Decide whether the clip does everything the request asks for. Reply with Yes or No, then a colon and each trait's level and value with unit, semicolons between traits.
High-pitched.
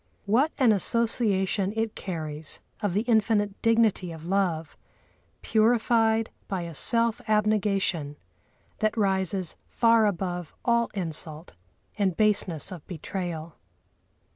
Yes: high, 200 Hz